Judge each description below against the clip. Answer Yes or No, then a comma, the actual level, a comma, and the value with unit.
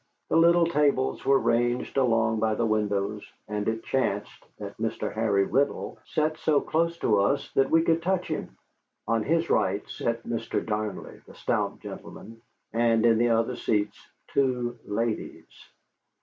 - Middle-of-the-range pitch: No, low, 115 Hz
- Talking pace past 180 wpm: No, average, 155 wpm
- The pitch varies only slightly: No, average, 4.5 semitones